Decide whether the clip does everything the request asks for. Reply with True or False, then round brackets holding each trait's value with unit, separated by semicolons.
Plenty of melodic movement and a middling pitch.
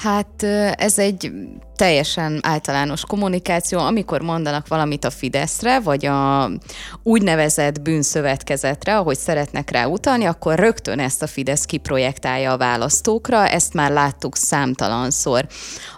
True (6.1 semitones; 155 Hz)